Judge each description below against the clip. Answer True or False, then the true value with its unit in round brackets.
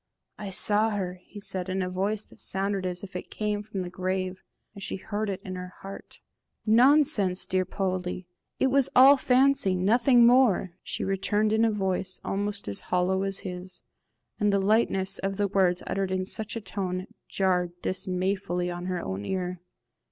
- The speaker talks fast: False (180 wpm)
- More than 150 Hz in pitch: True (190 Hz)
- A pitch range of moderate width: False (2.3 semitones)